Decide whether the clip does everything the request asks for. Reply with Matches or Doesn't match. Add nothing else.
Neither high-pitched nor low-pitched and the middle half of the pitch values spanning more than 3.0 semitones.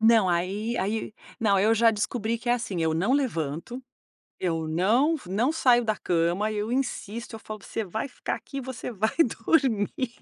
Doesn't match